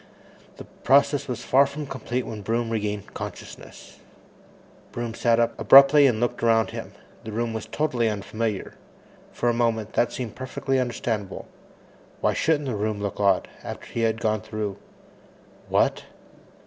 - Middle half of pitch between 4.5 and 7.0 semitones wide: No, average, 2.9 semitones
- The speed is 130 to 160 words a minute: Yes, average, 150 wpm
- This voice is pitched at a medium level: No, low, 115 Hz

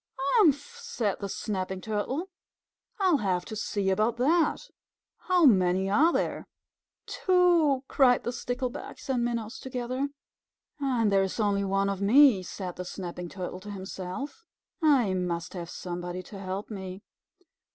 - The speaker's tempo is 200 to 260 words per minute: No, average, 140 wpm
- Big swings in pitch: Yes, wide, 6.3 semitones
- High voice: Yes, high, 210 Hz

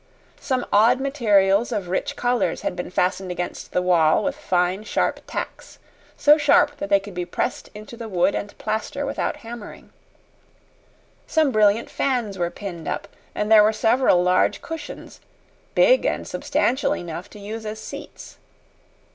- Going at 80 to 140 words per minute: No, average, 155 wpm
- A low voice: No, high, 210 Hz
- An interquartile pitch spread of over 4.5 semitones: Yes, average, 5.1 semitones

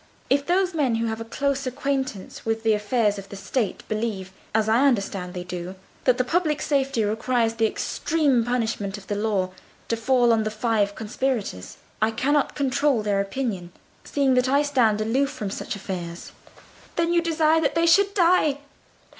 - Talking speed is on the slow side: No, average, 180 wpm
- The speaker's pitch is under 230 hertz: No, high, 235 Hz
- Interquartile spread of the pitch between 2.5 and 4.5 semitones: No, average, 5.1 semitones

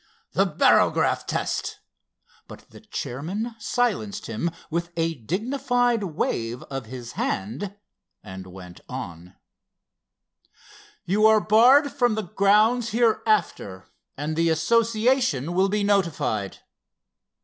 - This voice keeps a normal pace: No, slow, 105 wpm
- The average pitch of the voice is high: Yes, high, 195 Hz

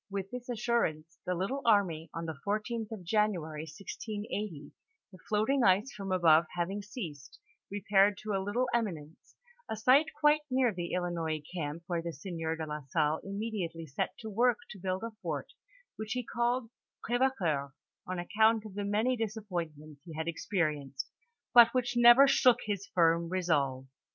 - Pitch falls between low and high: No, high, 195 Hz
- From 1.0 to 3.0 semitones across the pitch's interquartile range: No, average, 5.3 semitones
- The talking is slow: No, average, 165 wpm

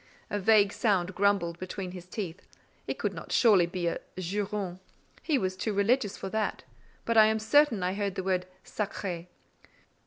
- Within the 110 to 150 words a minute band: No, average, 175 wpm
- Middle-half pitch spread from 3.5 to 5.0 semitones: No, average, 2.7 semitones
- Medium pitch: No, high, 195 Hz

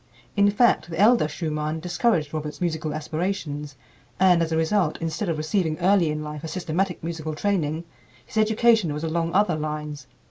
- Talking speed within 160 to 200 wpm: Yes, average, 170 wpm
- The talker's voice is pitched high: No, medium, 160 Hz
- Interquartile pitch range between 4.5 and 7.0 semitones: No, average, 3.7 semitones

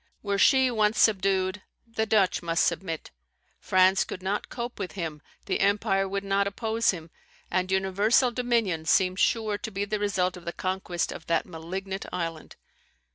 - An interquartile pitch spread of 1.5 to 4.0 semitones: Yes, narrow, 2.6 semitones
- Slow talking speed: No, average, 165 wpm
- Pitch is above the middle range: Yes, high, 195 Hz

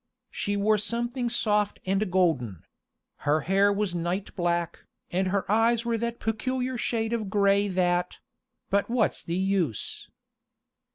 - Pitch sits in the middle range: No, high, 200 Hz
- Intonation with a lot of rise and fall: No, average, 3.8 semitones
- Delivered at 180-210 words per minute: No, slow, 135 wpm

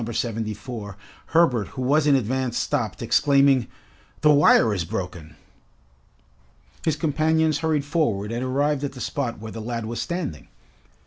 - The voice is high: No, low, 130 Hz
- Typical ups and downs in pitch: Yes, average, 5.0 semitones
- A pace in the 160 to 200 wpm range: No, average, 140 wpm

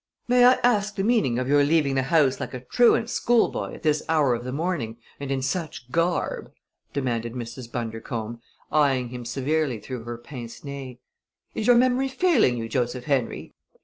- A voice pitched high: No, low, 135 Hz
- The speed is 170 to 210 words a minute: Yes, average, 180 wpm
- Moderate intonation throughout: No, wide, 5.7 semitones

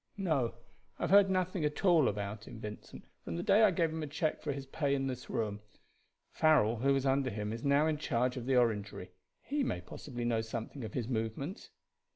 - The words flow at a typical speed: No, fast, 215 wpm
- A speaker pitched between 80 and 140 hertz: Yes, low, 135 Hz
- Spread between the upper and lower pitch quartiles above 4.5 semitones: Yes, wide, 5.6 semitones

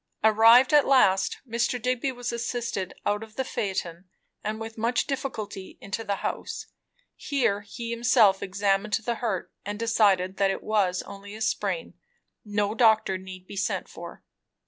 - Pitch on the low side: No, high, 215 Hz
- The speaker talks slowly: No, average, 155 wpm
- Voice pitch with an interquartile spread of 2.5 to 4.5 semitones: Yes, average, 3.0 semitones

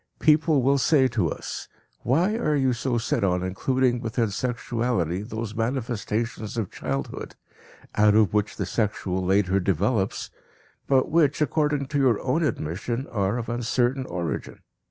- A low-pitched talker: Yes, low, 115 Hz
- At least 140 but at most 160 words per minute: Yes, average, 145 wpm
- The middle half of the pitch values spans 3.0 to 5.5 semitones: Yes, average, 4.6 semitones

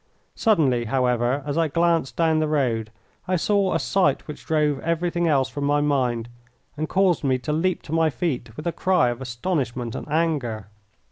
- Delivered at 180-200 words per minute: Yes, average, 185 wpm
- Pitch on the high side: No, medium, 150 Hz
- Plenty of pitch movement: No, average, 4.8 semitones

